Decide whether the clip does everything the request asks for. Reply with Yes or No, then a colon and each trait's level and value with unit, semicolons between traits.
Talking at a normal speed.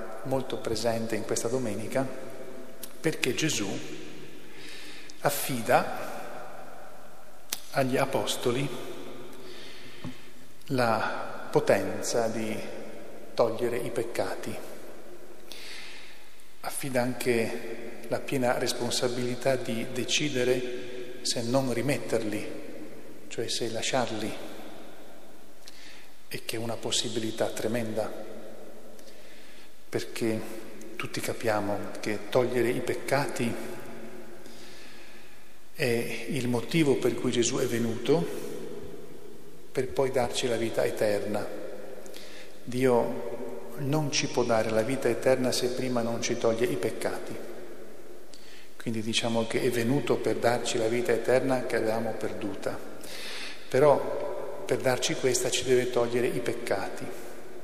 No: slow, 95 wpm